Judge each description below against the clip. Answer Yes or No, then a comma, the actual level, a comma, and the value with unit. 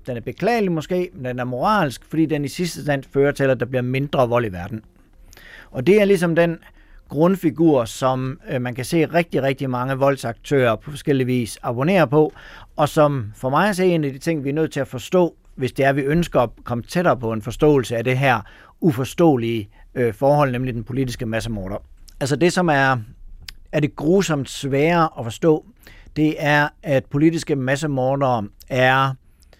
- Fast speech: No, average, 190 wpm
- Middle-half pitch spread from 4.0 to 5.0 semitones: Yes, average, 4.3 semitones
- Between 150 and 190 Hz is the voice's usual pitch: No, low, 135 Hz